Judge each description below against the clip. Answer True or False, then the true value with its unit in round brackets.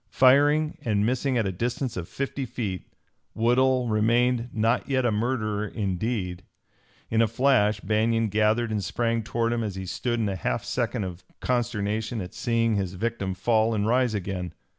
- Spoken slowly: False (175 wpm)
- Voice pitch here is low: True (115 Hz)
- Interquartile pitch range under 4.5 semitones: True (3.0 semitones)